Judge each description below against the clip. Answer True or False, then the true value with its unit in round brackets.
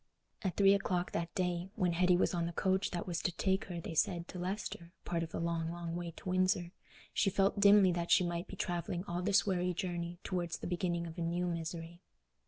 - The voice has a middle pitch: True (175 Hz)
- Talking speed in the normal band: False (210 wpm)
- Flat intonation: True (1.5 semitones)